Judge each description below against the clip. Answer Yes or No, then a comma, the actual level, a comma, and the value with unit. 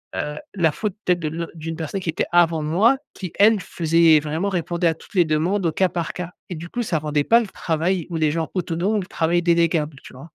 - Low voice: No, medium, 170 Hz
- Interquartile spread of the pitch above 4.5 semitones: No, narrow, 2.4 semitones